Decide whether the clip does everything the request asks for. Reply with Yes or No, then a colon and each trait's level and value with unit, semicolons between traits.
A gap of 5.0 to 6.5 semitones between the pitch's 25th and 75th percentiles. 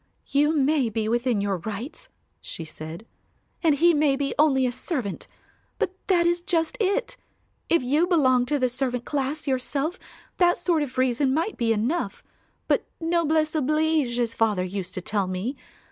Yes: average, 5.3 semitones